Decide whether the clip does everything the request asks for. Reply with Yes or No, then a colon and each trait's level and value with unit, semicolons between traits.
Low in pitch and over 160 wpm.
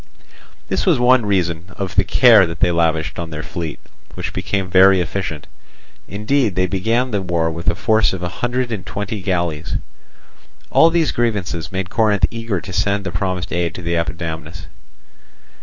Yes: very low, 95 Hz; average, 170 wpm